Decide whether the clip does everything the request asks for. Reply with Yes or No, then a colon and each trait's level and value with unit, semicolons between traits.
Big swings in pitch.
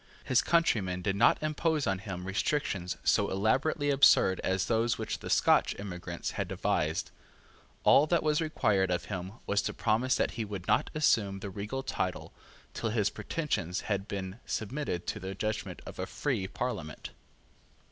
Yes: wide, 5.7 semitones